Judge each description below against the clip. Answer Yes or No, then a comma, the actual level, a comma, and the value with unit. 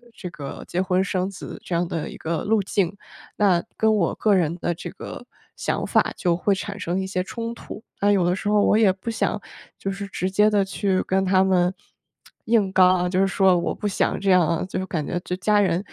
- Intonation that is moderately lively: No, narrow, 2.2 semitones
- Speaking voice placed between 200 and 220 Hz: No, high, 190 Hz